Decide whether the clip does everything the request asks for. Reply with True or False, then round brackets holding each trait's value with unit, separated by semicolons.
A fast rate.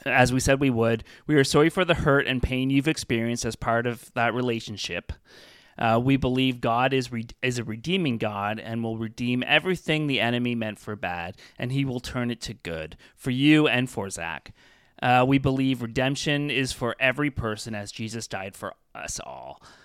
False (195 wpm)